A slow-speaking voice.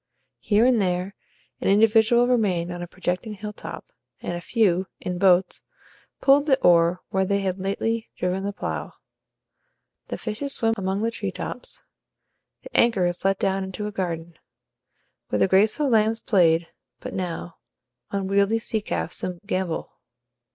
No: average, 150 wpm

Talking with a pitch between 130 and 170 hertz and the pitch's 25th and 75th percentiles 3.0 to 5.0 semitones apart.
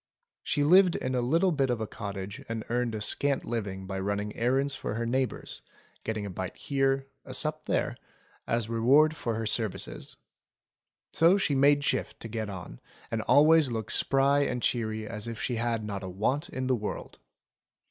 No: low, 120 Hz; average, 4.3 semitones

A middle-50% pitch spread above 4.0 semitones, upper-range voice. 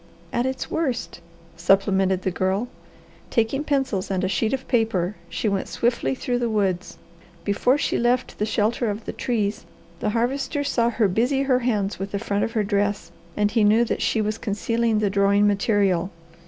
No: average, 3.3 semitones; high, 215 Hz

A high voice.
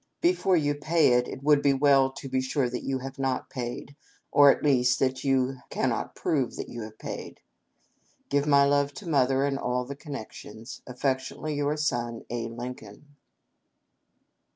No: low, 135 Hz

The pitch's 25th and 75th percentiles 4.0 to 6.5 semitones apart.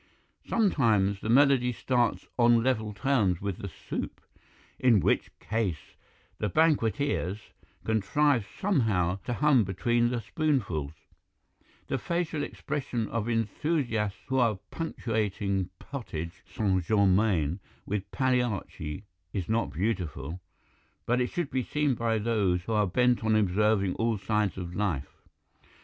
Yes: average, 4.4 semitones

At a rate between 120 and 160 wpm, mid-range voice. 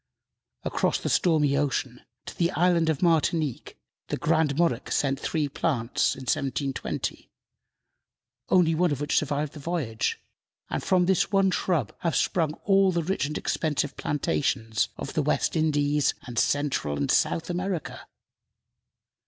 Yes: average, 145 wpm; medium, 150 Hz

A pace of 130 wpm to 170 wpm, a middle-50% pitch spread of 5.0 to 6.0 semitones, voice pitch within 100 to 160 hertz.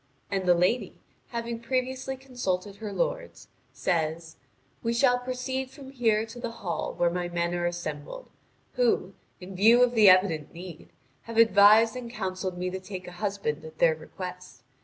No: average, 165 wpm; wide, 5.4 semitones; high, 200 Hz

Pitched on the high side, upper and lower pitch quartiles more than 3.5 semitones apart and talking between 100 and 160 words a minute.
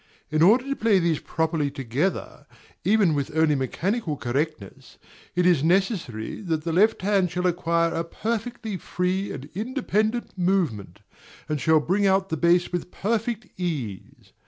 No: medium, 175 Hz; average, 4.5 semitones; average, 150 wpm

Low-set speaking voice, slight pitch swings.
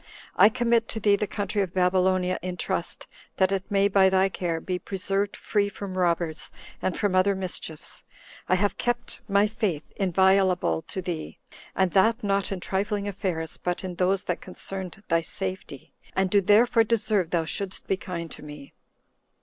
No: high, 190 Hz; narrow, 2.0 semitones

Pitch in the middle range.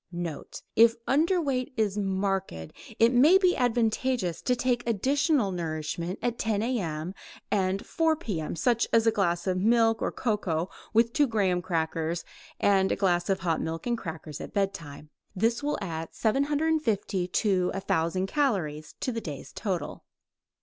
No: high, 200 Hz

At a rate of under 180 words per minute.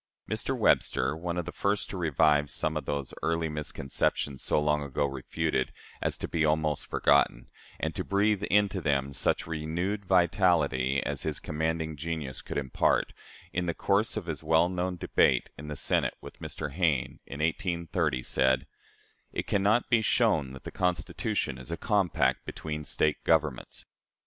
Yes: average, 165 wpm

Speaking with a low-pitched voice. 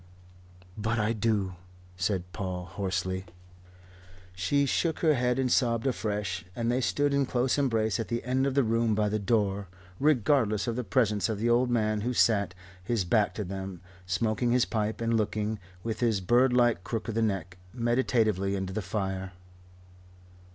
Yes: low, 110 Hz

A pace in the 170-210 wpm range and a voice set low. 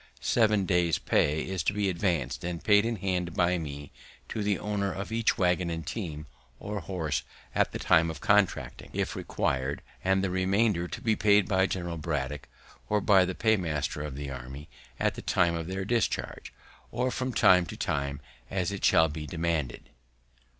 Yes: average, 180 wpm; very low, 90 Hz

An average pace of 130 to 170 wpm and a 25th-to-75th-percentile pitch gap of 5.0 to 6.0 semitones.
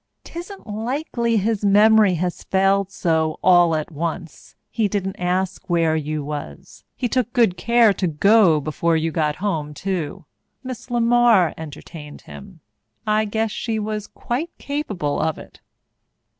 Yes: average, 145 wpm; wide, 5.5 semitones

